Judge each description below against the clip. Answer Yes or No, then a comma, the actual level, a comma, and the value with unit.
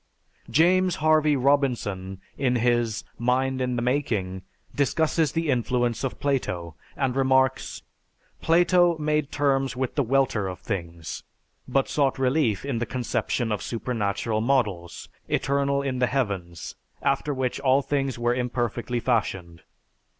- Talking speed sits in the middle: No, slow, 130 wpm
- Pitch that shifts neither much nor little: Yes, average, 3.6 semitones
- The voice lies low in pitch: Yes, low, 125 Hz